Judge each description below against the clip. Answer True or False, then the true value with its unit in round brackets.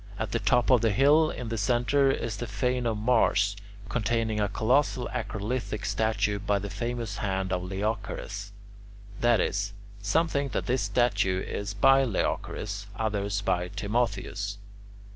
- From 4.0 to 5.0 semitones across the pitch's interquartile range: False (3.3 semitones)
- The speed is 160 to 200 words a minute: False (150 wpm)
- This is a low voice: True (110 Hz)